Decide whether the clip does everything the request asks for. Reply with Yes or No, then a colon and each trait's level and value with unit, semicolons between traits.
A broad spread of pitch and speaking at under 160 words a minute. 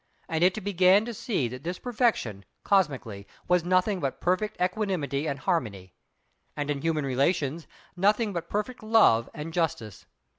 Yes: wide, 6.3 semitones; average, 150 wpm